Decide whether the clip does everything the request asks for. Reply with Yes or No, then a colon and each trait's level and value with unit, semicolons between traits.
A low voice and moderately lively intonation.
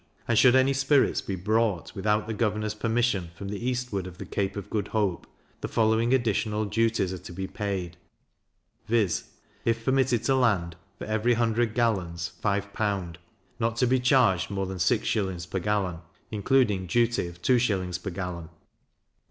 Yes: low, 105 Hz; average, 3.8 semitones